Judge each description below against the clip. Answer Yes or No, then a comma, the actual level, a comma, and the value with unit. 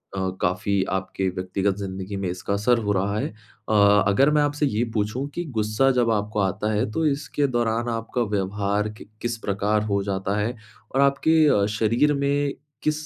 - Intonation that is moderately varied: Yes, average, 4.3 semitones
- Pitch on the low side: Yes, low, 105 Hz